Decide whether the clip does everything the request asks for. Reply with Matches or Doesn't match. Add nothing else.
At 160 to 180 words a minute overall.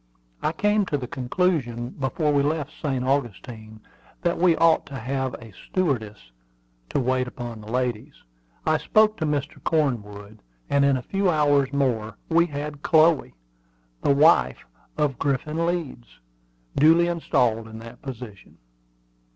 Doesn't match